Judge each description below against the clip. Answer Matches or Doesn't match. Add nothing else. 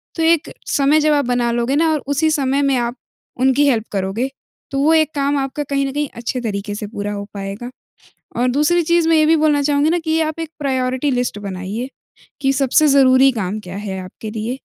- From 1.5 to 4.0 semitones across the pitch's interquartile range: Doesn't match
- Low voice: Doesn't match